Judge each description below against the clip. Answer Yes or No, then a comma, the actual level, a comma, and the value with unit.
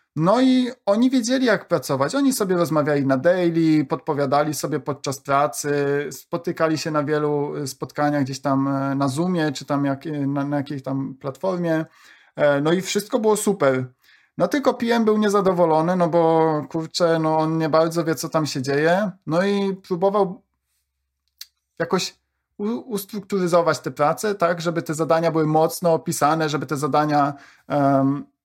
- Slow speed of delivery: No, average, 150 wpm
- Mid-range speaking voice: Yes, medium, 160 Hz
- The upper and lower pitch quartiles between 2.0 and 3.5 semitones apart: No, average, 4.0 semitones